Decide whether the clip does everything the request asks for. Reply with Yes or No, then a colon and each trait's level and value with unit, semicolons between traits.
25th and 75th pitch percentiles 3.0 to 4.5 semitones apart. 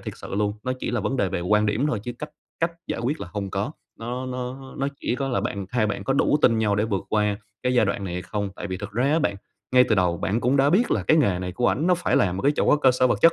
No: average, 4.9 semitones